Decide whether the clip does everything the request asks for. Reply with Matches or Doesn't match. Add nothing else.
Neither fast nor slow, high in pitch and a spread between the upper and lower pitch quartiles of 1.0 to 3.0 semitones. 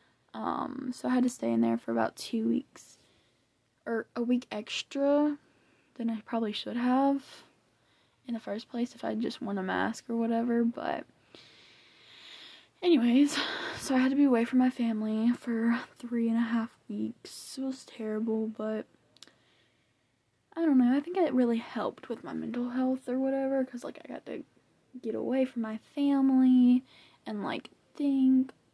Matches